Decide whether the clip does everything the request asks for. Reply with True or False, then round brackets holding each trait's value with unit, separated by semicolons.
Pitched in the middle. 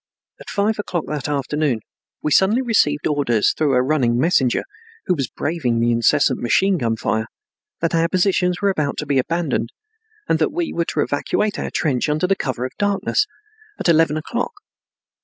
True (150 Hz)